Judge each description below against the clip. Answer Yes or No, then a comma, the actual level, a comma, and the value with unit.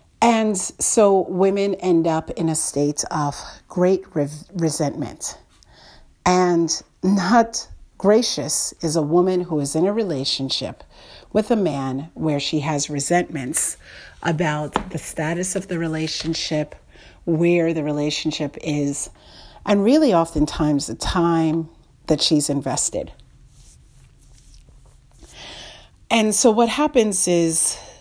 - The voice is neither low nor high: Yes, medium, 165 Hz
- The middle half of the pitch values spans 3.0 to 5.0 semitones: Yes, average, 4.1 semitones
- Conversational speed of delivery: No, slow, 115 wpm